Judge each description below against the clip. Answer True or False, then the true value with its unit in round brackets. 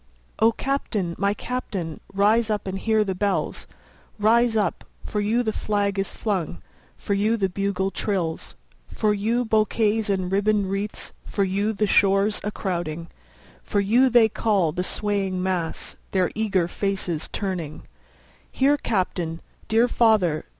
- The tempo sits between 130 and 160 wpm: True (135 wpm)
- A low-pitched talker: False (200 Hz)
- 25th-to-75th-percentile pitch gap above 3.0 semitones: False (2.7 semitones)